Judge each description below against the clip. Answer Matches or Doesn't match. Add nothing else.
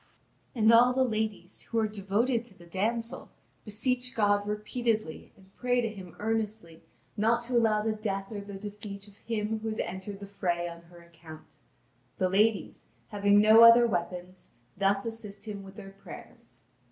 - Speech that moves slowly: Doesn't match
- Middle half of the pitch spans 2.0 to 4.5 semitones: Matches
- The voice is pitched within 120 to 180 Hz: Doesn't match